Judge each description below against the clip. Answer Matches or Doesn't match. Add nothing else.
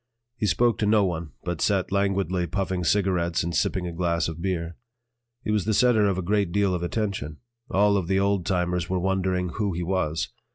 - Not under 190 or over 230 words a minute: Matches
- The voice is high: Doesn't match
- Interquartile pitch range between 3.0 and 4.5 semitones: Doesn't match